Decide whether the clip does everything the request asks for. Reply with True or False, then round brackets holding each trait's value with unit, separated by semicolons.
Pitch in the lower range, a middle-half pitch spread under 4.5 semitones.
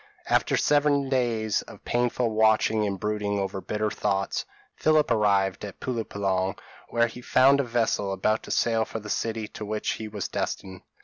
True (110 Hz; 2.7 semitones)